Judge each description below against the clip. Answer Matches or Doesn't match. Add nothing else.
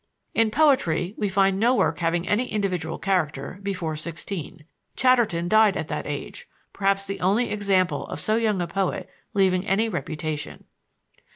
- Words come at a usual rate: Matches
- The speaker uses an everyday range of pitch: Matches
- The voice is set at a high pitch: Matches